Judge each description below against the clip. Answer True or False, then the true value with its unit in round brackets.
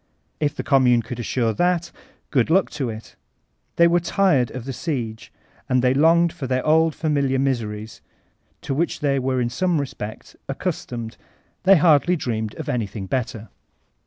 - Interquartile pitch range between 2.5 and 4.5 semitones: False (5.3 semitones)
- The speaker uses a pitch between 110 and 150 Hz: True (135 Hz)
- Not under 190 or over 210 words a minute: False (165 wpm)